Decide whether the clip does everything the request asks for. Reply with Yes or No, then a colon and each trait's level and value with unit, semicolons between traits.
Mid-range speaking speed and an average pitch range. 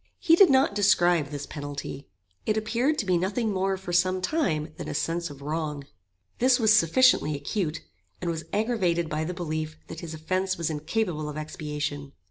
Yes: average, 180 wpm; average, 5.0 semitones